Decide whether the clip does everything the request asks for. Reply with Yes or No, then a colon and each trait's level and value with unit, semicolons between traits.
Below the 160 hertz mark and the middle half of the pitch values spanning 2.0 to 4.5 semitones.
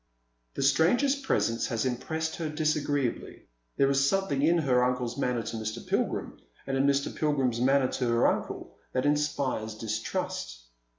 Yes: low, 135 Hz; average, 3.9 semitones